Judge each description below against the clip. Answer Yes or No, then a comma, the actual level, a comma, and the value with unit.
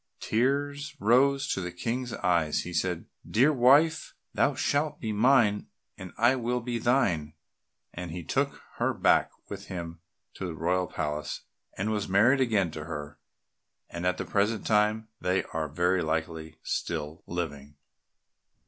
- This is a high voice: No, very low, 95 Hz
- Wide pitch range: Yes, wide, 6.5 semitones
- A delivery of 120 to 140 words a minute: No, average, 155 wpm